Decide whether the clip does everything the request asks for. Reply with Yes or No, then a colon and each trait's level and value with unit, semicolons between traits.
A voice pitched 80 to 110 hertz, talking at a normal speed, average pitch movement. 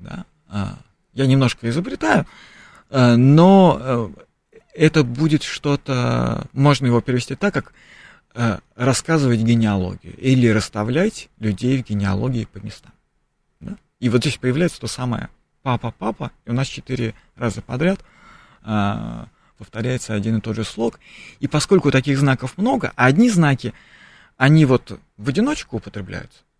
No: low, 125 Hz; average, 125 wpm; average, 4.5 semitones